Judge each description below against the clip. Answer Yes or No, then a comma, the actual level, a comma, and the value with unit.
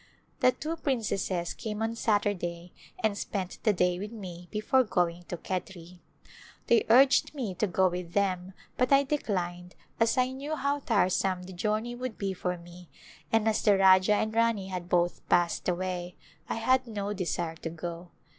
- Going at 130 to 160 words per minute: No, average, 175 wpm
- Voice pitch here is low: No, high, 195 Hz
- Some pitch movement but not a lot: Yes, average, 4.1 semitones